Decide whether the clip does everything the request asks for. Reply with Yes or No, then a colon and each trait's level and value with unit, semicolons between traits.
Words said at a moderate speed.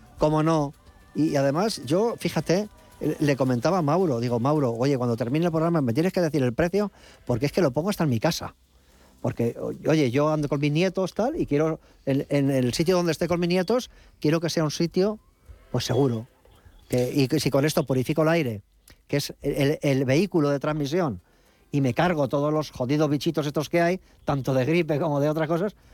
No: fast, 210 wpm